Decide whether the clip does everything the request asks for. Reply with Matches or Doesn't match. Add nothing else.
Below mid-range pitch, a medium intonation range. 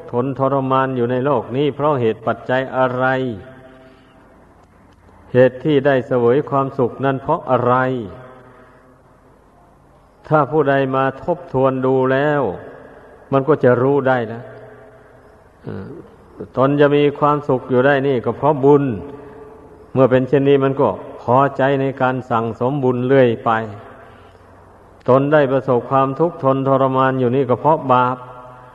Doesn't match